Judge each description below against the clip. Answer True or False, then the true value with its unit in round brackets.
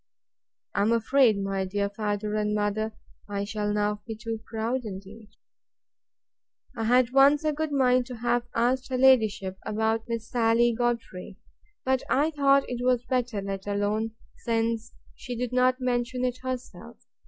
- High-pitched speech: True (230 Hz)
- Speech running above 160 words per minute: False (155 wpm)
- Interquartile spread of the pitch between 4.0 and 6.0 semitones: False (3.1 semitones)